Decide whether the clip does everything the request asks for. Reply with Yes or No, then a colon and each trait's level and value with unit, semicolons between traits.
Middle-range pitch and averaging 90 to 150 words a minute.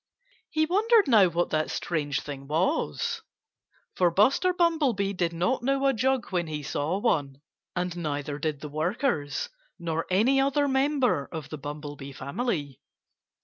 Yes: medium, 180 Hz; average, 145 wpm